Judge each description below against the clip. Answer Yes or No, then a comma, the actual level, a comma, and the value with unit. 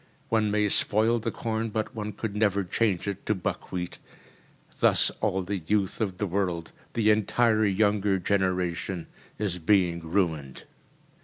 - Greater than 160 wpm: No, average, 145 wpm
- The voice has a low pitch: Yes, low, 100 Hz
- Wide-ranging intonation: No, average, 3.0 semitones